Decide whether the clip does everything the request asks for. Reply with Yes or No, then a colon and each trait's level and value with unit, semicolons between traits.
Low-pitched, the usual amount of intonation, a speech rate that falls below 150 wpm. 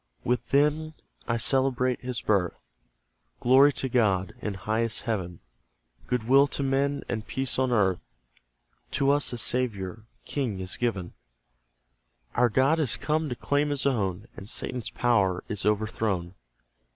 Yes: low, 120 Hz; average, 4.6 semitones; average, 140 wpm